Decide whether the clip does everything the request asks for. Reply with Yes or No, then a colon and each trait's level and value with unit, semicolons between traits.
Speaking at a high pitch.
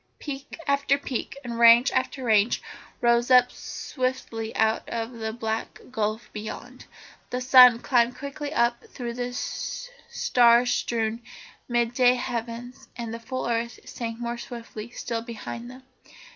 Yes: high, 240 Hz